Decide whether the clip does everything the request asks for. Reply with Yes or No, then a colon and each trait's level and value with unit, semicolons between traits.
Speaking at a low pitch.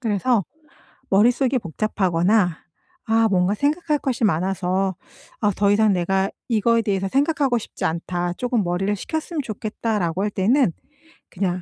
No: high, 205 Hz